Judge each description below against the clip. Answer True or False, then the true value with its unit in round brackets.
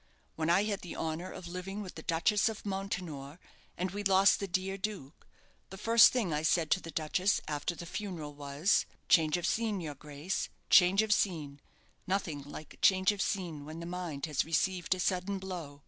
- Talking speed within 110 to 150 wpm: False (195 wpm)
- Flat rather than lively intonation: False (3.7 semitones)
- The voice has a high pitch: False (180 Hz)